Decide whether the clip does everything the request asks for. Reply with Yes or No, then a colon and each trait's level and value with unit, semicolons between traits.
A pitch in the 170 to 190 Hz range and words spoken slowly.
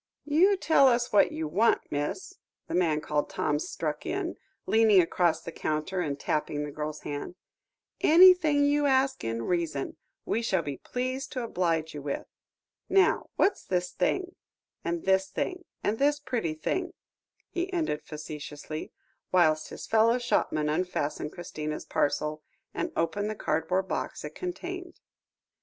No: medium, 185 Hz; average, 150 wpm